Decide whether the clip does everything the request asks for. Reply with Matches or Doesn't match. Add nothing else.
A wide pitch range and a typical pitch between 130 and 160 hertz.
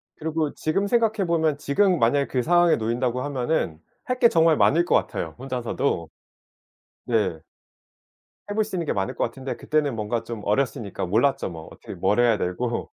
Matches